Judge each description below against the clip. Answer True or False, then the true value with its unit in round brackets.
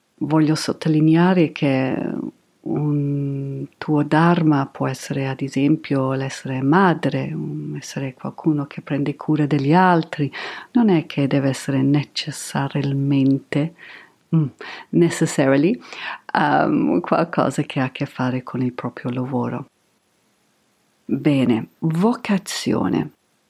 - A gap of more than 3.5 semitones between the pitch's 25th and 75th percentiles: False (2.8 semitones)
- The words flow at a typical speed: False (100 wpm)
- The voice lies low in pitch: False (145 Hz)